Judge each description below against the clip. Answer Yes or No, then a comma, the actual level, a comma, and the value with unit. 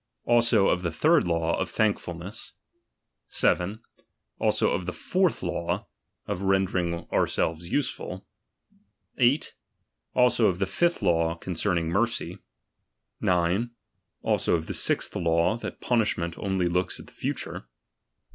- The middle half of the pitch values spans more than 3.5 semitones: Yes, average, 4.4 semitones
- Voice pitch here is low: Yes, very low, 90 Hz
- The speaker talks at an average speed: No, slow, 125 wpm